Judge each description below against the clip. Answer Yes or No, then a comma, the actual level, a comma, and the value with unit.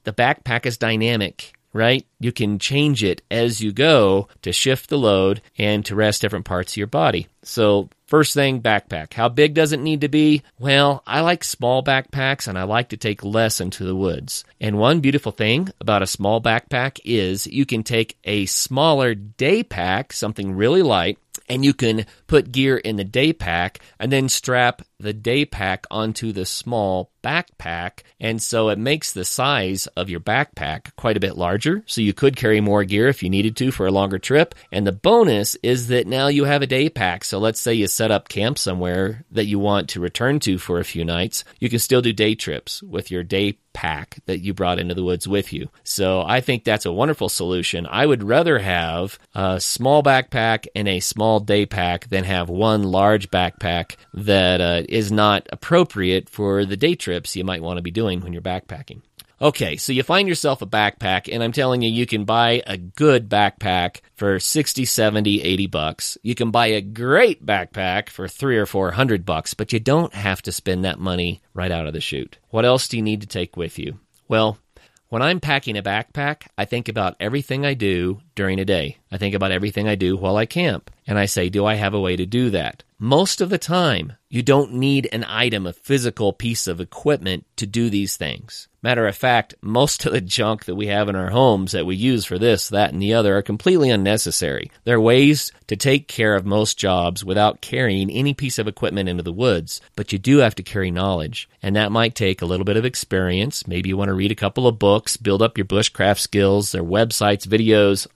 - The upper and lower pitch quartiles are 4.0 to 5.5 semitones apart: Yes, average, 4.4 semitones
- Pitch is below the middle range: Yes, low, 105 Hz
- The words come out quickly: Yes, fast, 215 wpm